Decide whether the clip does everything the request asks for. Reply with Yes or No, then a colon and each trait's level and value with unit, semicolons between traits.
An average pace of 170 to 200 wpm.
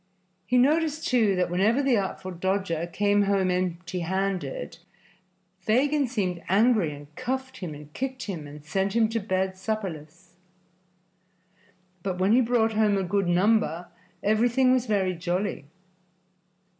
No: slow, 135 wpm